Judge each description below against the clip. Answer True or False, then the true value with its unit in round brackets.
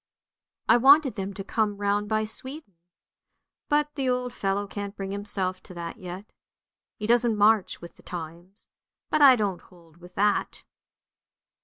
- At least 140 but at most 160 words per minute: True (155 wpm)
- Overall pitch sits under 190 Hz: False (205 Hz)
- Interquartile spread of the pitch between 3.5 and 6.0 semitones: True (4.1 semitones)